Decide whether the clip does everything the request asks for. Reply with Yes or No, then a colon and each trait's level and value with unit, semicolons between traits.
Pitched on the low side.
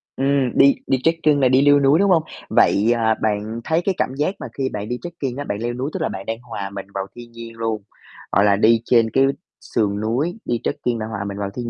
Yes: low, 120 Hz